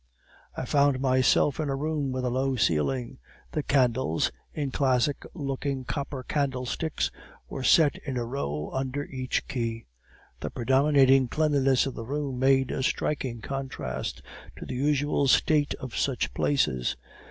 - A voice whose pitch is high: No, low, 135 Hz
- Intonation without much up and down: Yes, narrow, 2.2 semitones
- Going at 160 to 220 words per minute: No, average, 150 wpm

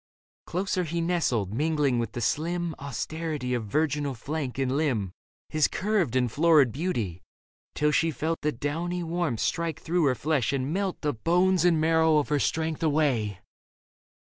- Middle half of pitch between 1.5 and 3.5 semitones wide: No, average, 4.4 semitones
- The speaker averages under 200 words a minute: Yes, average, 160 wpm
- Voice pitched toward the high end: No, medium, 155 Hz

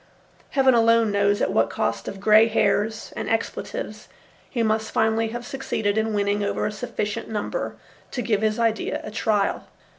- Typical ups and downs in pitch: No, narrow, 1.8 semitones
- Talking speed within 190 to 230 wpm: No, average, 170 wpm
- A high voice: Yes, high, 220 Hz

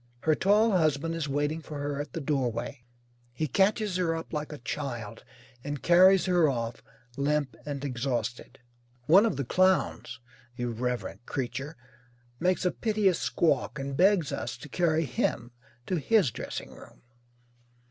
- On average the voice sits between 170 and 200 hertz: No, medium, 150 Hz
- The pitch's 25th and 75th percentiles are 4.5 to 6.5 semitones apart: Yes, wide, 5.4 semitones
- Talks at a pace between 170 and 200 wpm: No, average, 145 wpm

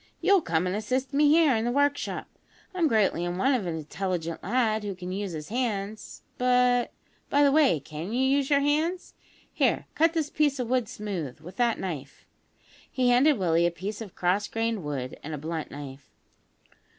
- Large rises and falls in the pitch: Yes, wide, 7.2 semitones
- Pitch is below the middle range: No, high, 220 Hz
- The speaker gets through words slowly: No, average, 190 wpm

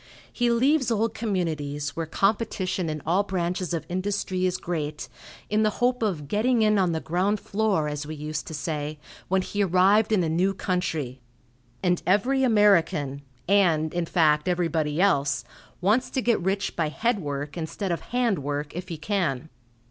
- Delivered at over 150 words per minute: Yes, average, 170 wpm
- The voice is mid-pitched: Yes, medium, 180 Hz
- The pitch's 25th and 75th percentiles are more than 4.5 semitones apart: Yes, average, 4.9 semitones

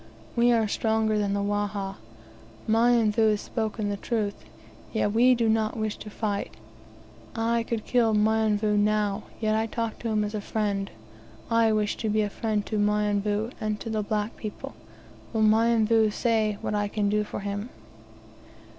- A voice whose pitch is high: Yes, high, 215 Hz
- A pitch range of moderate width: No, narrow, 1.4 semitones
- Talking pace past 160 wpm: Yes, average, 170 wpm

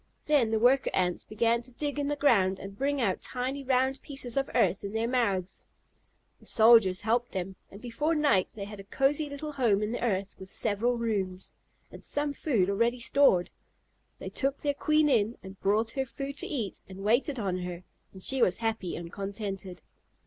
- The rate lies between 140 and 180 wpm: No, average, 195 wpm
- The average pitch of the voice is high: Yes, high, 230 Hz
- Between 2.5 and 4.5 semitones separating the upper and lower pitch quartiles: No, wide, 5.5 semitones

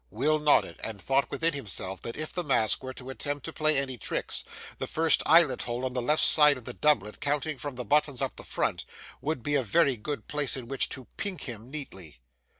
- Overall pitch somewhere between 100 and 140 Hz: Yes, low, 135 Hz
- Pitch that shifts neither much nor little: Yes, average, 3.5 semitones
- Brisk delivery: Yes, fast, 230 wpm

